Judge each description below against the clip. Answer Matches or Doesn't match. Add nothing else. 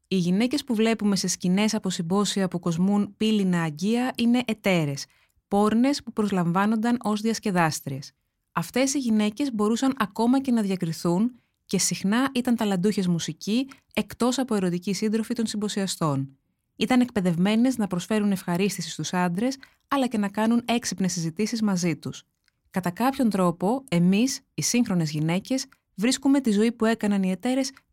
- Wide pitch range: Doesn't match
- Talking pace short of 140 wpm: Doesn't match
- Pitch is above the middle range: Matches